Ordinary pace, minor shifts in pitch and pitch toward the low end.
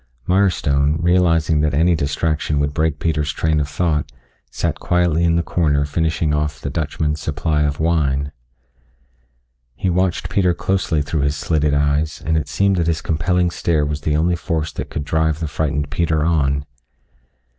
Yes: average, 165 wpm; narrow, 2.3 semitones; very low, 80 Hz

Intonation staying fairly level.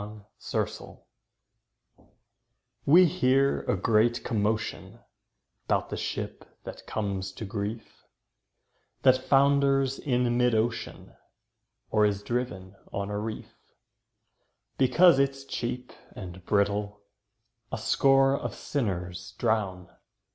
No: average, 4.8 semitones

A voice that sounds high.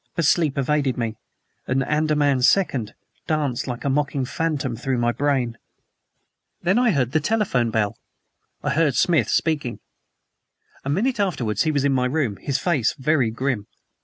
No: medium, 140 Hz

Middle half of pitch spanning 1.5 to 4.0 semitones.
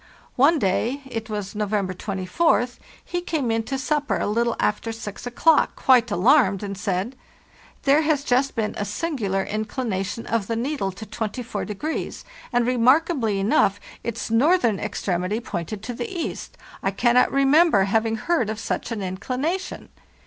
No: average, 5.0 semitones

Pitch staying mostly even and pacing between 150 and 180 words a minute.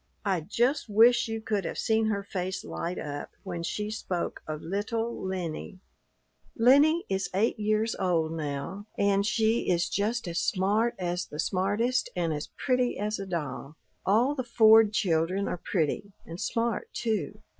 No: average, 4.3 semitones; average, 160 wpm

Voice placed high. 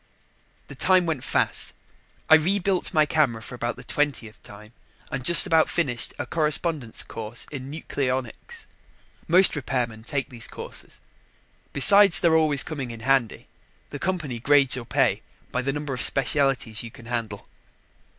No: low, 135 Hz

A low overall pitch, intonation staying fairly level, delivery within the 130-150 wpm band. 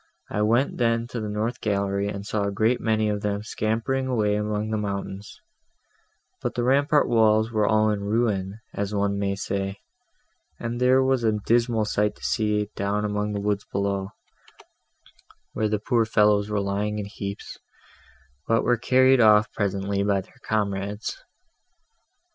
No: low, 105 Hz; narrow, 2.0 semitones; average, 160 wpm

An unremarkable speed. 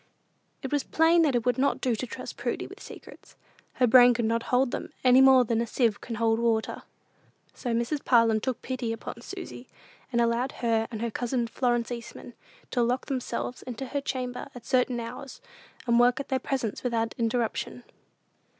Yes: average, 185 wpm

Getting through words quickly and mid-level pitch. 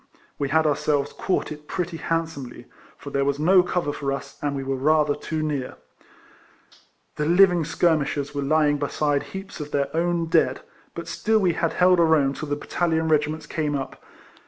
No: average, 190 wpm; medium, 150 Hz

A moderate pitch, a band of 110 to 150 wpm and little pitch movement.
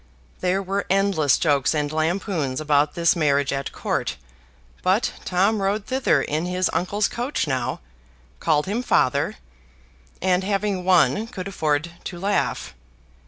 No: medium, 180 Hz; slow, 135 wpm; average, 4.8 semitones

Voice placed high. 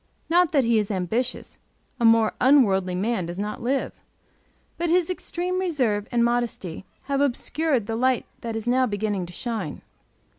Yes: high, 235 Hz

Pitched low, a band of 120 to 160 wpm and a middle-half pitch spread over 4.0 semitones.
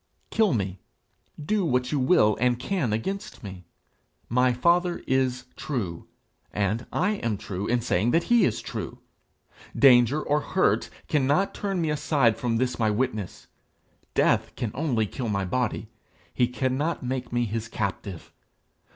Yes: low, 125 Hz; average, 150 wpm; average, 5.3 semitones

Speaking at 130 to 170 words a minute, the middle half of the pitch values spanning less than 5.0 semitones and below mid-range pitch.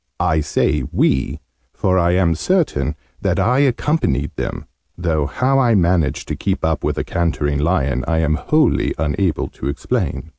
No: average, 160 wpm; average, 5.3 semitones; very low, 85 Hz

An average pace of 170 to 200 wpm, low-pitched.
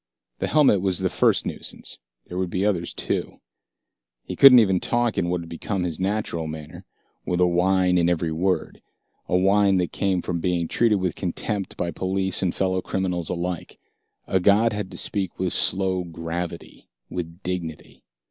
Yes: average, 175 wpm; very low, 90 Hz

